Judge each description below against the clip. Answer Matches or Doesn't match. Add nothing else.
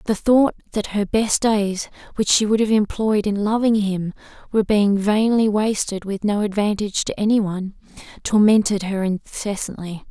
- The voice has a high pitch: Matches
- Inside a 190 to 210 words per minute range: Doesn't match